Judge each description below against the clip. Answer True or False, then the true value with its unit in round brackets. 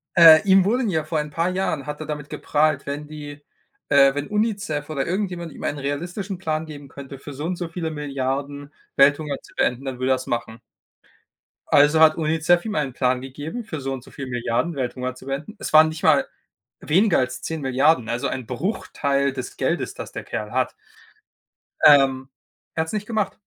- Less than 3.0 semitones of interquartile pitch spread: False (3.3 semitones)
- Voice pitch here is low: False (150 Hz)